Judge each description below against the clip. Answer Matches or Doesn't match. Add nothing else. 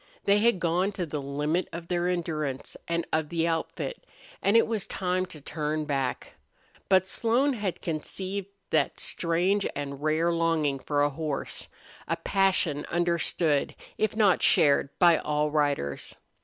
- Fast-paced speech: Doesn't match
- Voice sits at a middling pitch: Matches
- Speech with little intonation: Doesn't match